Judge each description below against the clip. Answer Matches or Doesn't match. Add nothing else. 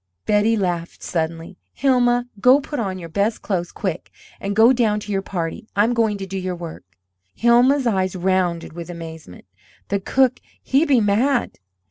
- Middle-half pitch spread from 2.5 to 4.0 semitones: Doesn't match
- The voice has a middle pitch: Doesn't match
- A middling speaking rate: Matches